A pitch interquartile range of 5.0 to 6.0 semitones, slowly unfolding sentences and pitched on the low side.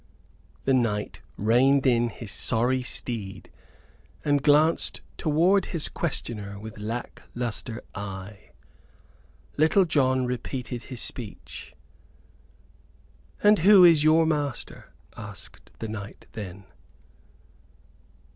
Yes: wide, 5.5 semitones; slow, 100 wpm; low, 125 Hz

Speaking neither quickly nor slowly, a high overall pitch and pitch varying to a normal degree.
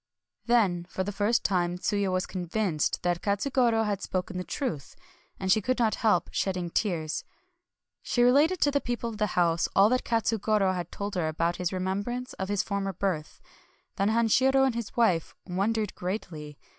Yes: average, 175 wpm; high, 200 Hz; average, 4.1 semitones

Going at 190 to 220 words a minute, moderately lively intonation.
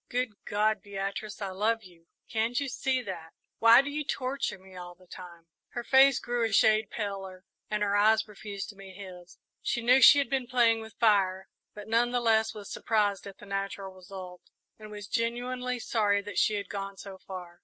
Yes: average, 200 wpm; average, 3.3 semitones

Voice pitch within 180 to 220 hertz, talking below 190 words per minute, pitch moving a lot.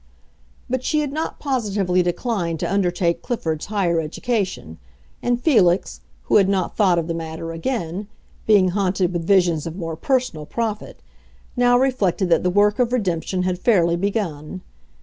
No: medium, 185 Hz; average, 155 wpm; average, 4.9 semitones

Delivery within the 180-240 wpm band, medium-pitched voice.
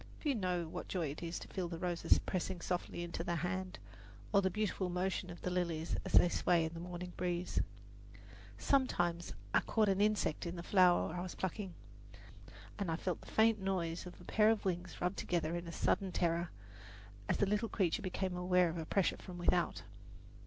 Yes: average, 200 wpm; medium, 180 Hz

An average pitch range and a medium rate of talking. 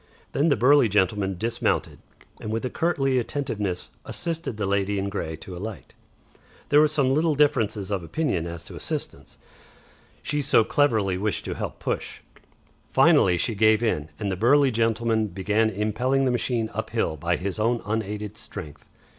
Yes: average, 4.8 semitones; average, 165 wpm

